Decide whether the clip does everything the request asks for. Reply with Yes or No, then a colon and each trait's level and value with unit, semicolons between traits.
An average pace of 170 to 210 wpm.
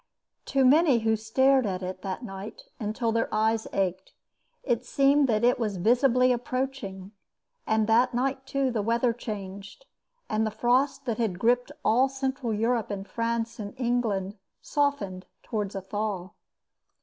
No: average, 150 wpm